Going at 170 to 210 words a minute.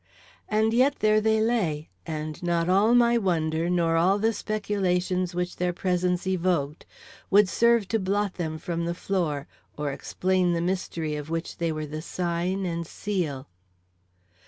No: average, 160 wpm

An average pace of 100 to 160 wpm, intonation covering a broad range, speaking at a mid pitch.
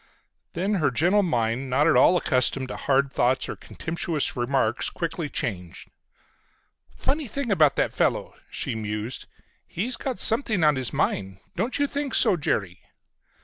Yes: average, 150 wpm; wide, 8.3 semitones; medium, 145 Hz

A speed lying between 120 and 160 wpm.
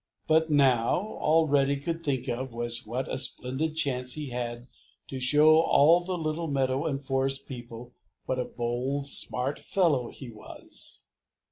Yes: average, 155 wpm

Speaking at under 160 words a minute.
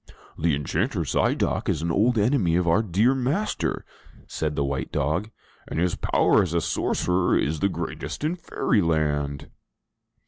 Yes: average, 150 wpm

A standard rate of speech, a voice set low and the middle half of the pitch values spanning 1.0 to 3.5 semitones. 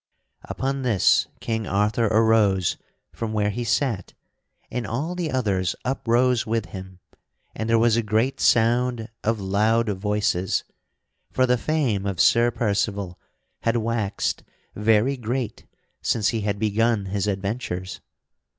No: slow, 130 wpm; low, 110 Hz; average, 2.8 semitones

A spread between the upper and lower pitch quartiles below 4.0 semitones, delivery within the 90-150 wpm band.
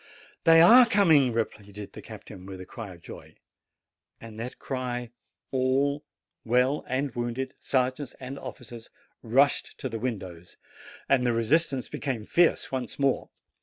Yes: average, 3.3 semitones; average, 140 wpm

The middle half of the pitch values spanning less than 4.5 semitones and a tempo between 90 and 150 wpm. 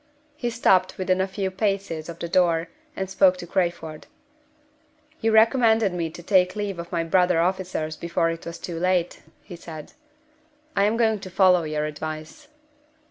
No: average, 2.7 semitones; average, 170 wpm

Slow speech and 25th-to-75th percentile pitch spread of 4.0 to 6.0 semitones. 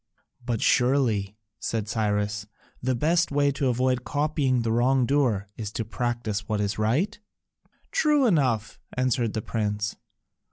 Yes: slow, 130 wpm; average, 4.3 semitones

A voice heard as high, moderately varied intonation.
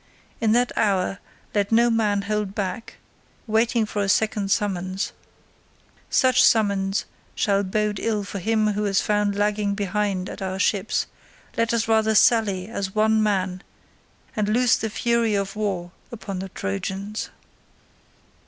No: high, 210 Hz; narrow, 2.0 semitones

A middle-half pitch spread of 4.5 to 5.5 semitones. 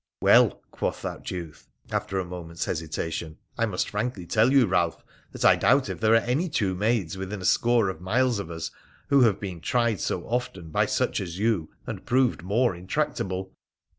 Yes: average, 5.1 semitones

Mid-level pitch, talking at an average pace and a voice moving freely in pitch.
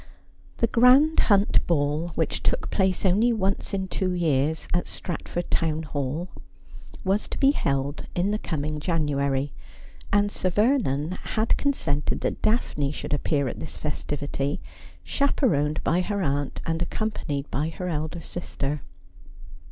Yes: medium, 165 Hz; average, 145 wpm; wide, 5.7 semitones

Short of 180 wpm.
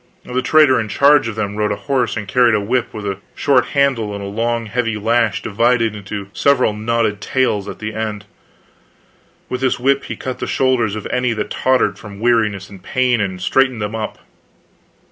No: average, 195 wpm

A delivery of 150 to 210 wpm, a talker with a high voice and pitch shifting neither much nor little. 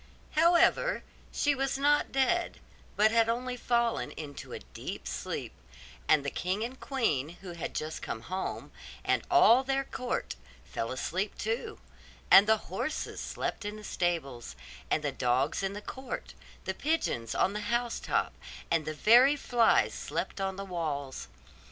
No: average, 160 wpm; high, 210 Hz; wide, 8.4 semitones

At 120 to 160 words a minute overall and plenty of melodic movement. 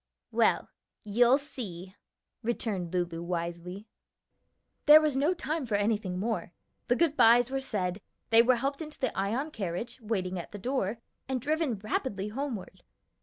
Yes: average, 150 wpm; wide, 5.9 semitones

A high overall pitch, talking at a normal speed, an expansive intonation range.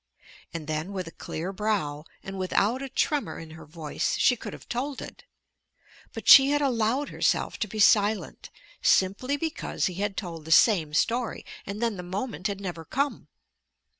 Yes: high, 200 Hz; average, 175 wpm; wide, 6.2 semitones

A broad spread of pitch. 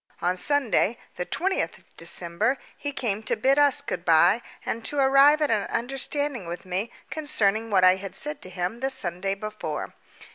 Yes: wide, 6.9 semitones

